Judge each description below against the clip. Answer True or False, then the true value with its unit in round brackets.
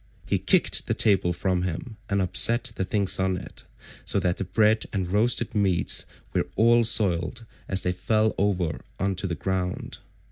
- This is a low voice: True (95 Hz)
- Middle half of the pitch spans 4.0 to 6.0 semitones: False (3.1 semitones)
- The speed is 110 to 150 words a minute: False (175 wpm)